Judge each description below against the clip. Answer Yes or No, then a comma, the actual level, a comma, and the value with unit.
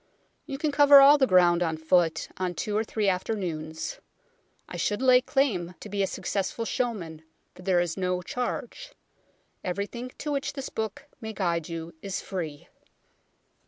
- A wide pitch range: Yes, wide, 6.2 semitones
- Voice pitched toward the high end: Yes, high, 195 Hz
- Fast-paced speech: No, average, 160 wpm